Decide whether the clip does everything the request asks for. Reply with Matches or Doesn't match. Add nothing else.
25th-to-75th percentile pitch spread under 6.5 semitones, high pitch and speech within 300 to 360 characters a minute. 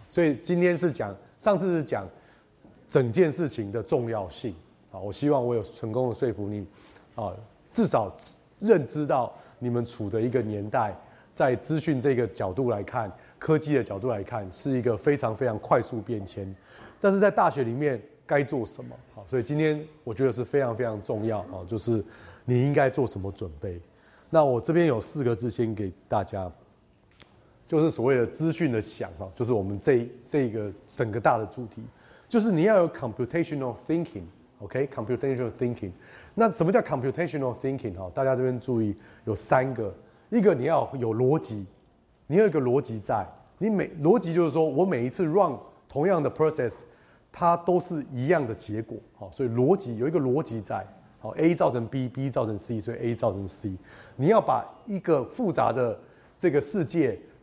Doesn't match